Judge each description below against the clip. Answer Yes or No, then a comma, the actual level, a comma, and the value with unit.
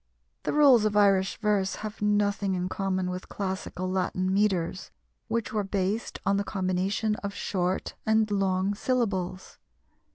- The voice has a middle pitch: No, high, 195 Hz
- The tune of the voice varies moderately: No, narrow, 2.1 semitones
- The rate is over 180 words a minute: No, average, 140 wpm